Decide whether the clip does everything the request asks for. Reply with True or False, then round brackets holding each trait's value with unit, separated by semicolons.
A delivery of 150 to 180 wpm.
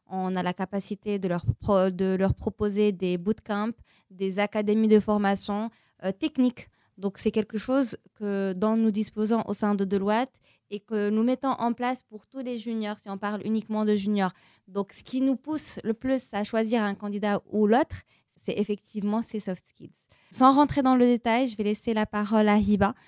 False (200 wpm)